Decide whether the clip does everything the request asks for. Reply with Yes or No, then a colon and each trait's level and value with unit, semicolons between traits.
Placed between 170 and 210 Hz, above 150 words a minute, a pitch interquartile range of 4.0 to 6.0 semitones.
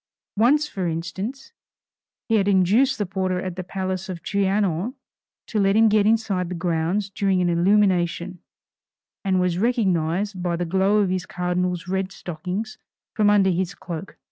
No: high, 190 Hz; average, 165 wpm; narrow, 2.6 semitones